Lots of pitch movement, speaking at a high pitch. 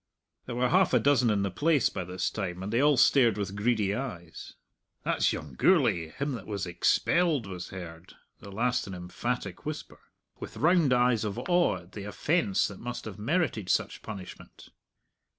No: wide, 5.9 semitones; low, 110 Hz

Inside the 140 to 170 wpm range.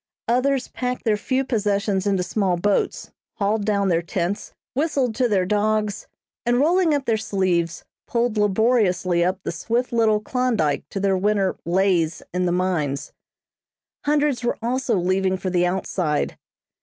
Yes: average, 150 wpm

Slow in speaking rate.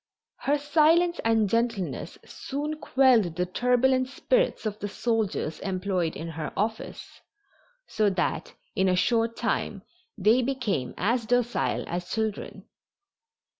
Yes: slow, 125 wpm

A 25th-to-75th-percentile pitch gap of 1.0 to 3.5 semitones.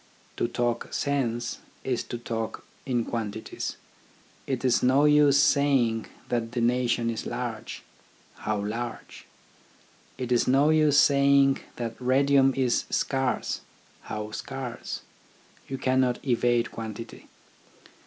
Yes: narrow, 2.6 semitones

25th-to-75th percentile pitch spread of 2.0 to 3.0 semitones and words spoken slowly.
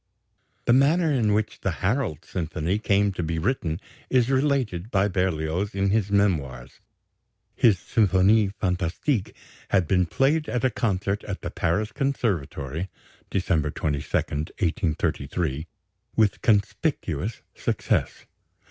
No: average, 5.1 semitones; slow, 120 wpm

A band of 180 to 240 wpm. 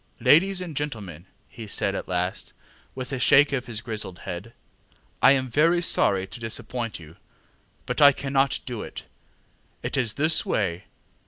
No: average, 160 wpm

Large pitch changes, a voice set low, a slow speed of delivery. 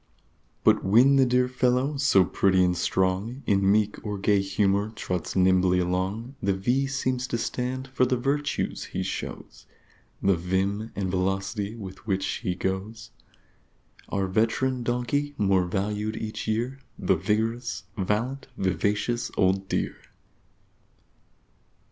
No: average, 4.4 semitones; low, 105 Hz; slow, 130 wpm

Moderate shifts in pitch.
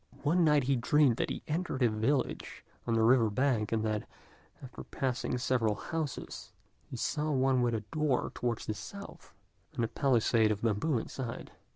Yes: average, 4.0 semitones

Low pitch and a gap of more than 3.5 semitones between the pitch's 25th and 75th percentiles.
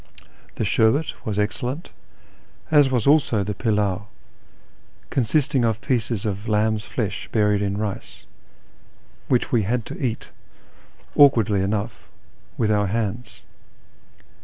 No: low, 110 Hz; average, 3.0 semitones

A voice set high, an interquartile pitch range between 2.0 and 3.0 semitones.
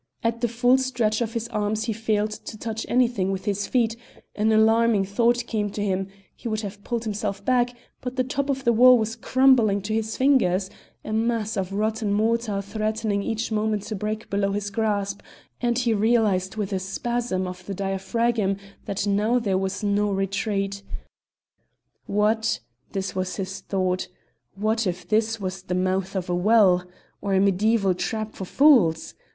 Yes: high, 215 Hz; average, 2.7 semitones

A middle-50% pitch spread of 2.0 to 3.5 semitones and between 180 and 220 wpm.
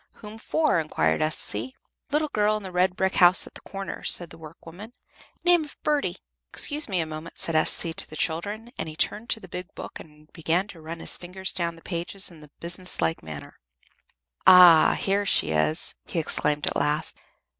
No: average, 3.9 semitones; average, 200 wpm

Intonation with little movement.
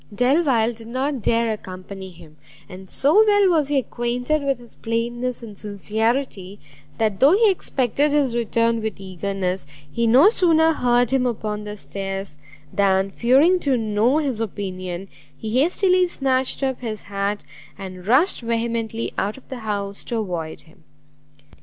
No: average, 5.0 semitones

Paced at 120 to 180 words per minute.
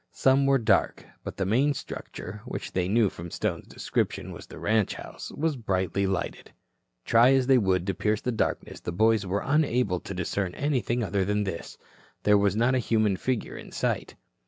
No: average, 190 wpm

